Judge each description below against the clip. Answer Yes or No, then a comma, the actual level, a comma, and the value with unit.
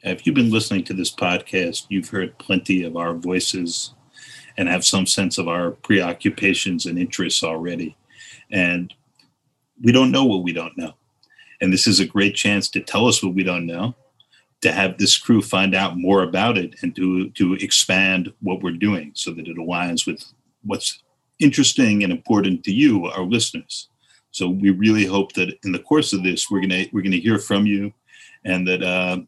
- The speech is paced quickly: No, average, 195 wpm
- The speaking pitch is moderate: No, very low, 95 Hz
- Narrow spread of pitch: Yes, narrow, 2.2 semitones